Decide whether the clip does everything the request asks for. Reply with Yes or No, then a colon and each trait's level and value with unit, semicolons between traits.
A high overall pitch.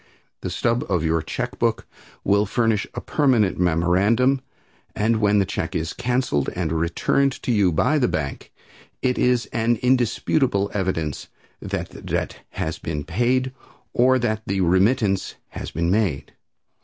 No: low, 105 Hz